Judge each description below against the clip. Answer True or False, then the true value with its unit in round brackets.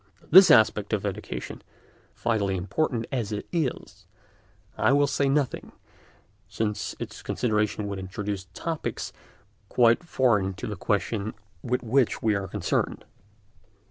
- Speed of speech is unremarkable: False (130 wpm)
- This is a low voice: True (110 Hz)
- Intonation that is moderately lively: True (4.1 semitones)